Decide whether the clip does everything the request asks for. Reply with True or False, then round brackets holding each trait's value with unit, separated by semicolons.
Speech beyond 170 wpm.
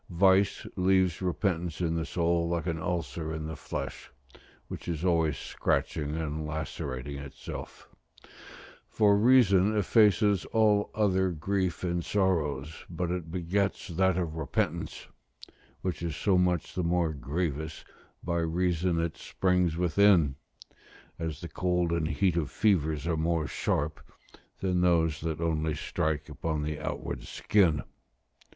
False (135 wpm)